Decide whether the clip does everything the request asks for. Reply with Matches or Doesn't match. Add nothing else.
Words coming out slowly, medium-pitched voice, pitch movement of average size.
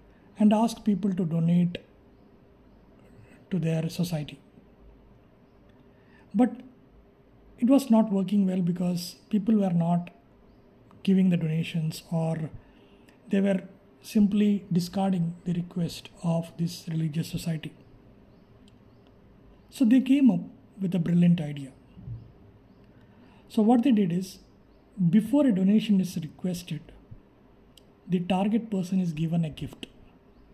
Matches